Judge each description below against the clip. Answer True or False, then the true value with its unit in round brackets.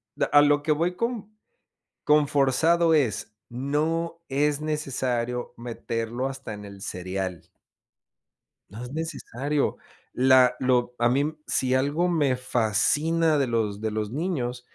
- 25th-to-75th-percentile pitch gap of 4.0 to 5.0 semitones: True (4.3 semitones)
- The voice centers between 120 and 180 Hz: True (135 Hz)